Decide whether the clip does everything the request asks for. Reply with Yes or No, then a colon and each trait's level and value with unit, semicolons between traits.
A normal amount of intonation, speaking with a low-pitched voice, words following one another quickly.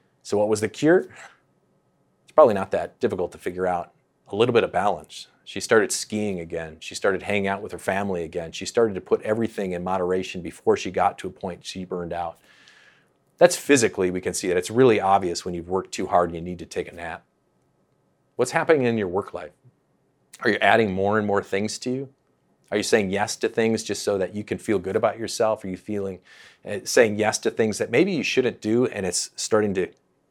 Yes: average, 3.2 semitones; very low, 95 Hz; fast, 225 wpm